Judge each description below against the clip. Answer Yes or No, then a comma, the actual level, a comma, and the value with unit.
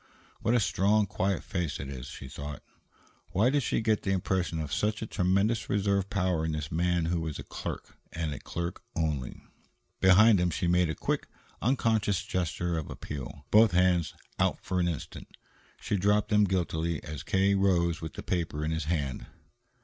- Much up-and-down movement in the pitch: No, average, 3.8 semitones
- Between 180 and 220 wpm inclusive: Yes, average, 185 wpm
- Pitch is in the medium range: No, very low, 90 Hz